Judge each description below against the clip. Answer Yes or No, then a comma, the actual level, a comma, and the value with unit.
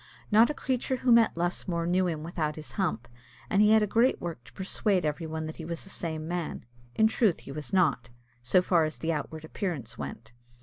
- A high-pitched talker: No, medium, 170 Hz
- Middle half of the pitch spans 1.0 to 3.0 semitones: No, average, 4.2 semitones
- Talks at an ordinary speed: No, fast, 220 wpm